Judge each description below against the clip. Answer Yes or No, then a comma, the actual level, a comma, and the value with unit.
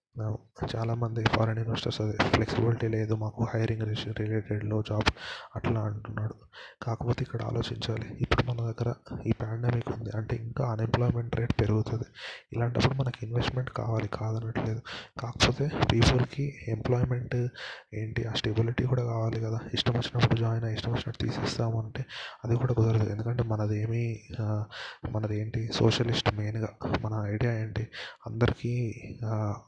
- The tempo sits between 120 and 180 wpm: Yes, fast, 125 wpm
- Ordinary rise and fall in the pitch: No, narrow, 1.7 semitones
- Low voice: Yes, low, 115 Hz